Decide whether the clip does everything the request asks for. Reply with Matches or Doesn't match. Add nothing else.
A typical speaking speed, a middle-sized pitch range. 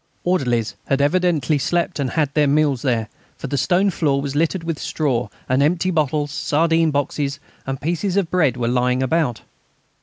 Matches